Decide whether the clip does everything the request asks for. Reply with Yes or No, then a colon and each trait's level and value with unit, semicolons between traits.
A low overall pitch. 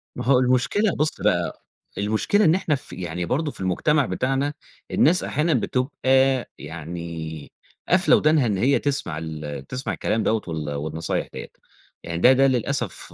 Yes: low, 125 Hz